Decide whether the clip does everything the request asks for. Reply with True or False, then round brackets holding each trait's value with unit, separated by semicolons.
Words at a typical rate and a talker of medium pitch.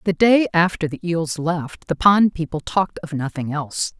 True (195 wpm; 165 Hz)